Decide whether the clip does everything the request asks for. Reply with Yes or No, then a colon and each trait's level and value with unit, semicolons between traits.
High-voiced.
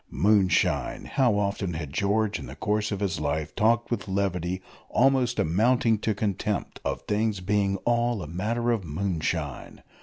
No: low, 100 Hz